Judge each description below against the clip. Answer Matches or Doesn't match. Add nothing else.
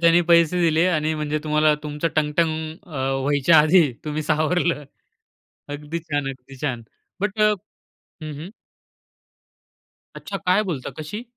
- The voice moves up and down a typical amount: Doesn't match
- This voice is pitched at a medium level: Matches